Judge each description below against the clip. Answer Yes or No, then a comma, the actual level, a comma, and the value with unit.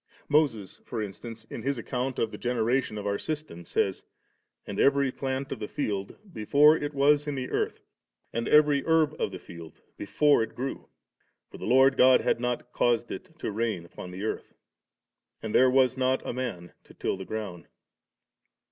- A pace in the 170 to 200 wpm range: Yes, average, 185 wpm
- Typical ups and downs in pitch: Yes, average, 4.5 semitones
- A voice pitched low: Yes, low, 125 Hz